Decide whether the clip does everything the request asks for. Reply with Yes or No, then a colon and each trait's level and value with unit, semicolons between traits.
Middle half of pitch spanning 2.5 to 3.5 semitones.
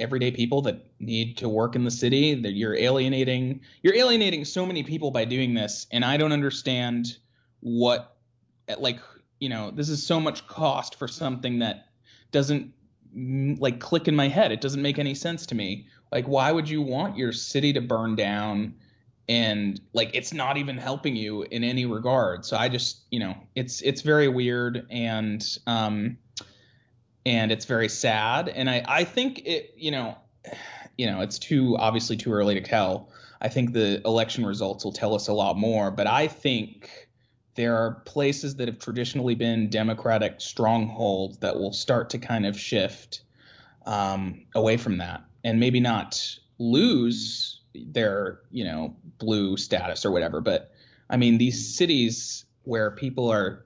Yes: average, 3.1 semitones